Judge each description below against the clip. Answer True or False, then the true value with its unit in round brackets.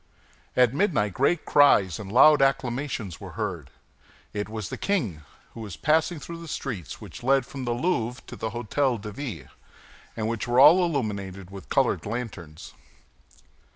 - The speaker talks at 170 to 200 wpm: False (160 wpm)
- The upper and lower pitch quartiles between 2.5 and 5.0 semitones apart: False (5.6 semitones)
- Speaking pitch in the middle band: False (120 Hz)